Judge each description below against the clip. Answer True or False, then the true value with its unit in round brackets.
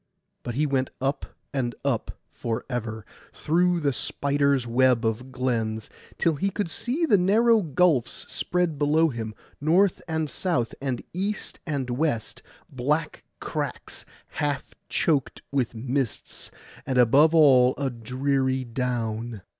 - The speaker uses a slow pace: True (130 wpm)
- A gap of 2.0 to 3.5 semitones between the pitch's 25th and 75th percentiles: False (4.6 semitones)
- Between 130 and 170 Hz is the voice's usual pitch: True (135 Hz)